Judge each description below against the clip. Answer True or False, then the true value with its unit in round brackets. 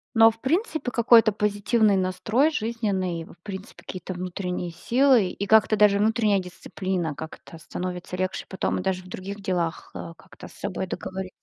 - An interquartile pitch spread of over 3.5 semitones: False (3.2 semitones)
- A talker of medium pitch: False (195 Hz)